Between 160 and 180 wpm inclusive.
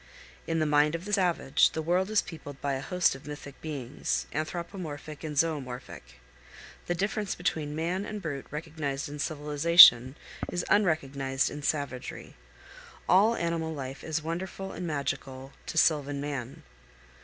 No: average, 145 wpm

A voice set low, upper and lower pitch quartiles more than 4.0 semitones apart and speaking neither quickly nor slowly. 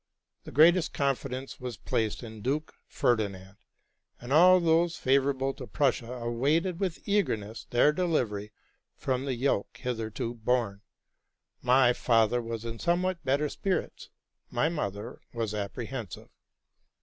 No: low, 125 Hz; average, 4.9 semitones; slow, 125 wpm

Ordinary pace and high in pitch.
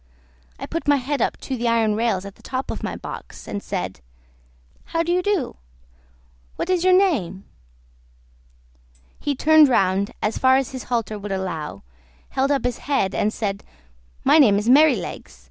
Yes: average, 175 wpm; high, 245 Hz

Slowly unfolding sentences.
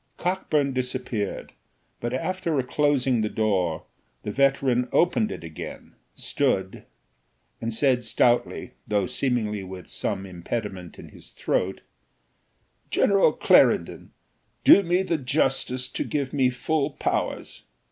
Yes: slow, 115 wpm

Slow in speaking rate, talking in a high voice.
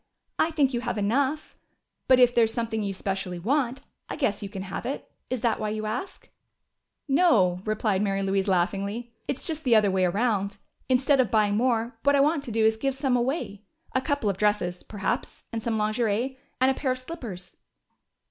No: fast, 205 wpm; high, 225 Hz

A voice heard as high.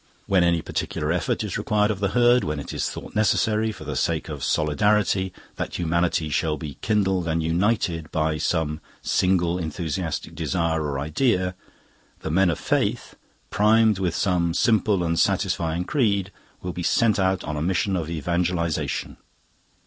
No: very low, 90 Hz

